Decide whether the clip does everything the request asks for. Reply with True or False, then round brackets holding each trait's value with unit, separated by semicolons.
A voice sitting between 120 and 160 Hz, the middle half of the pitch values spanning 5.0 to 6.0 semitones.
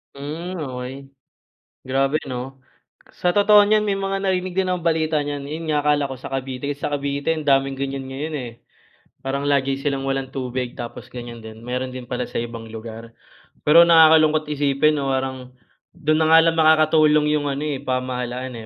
False (140 Hz; 3.2 semitones)